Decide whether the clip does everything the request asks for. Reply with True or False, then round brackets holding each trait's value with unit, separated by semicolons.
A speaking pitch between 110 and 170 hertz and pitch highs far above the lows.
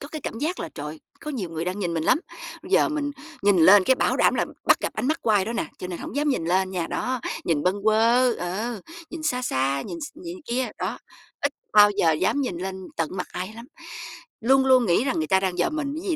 False (215 Hz; 6.9 semitones)